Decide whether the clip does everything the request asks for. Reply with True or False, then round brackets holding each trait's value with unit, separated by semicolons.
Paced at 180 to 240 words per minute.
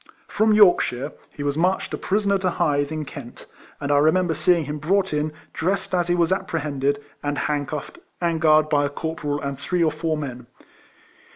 True (190 wpm)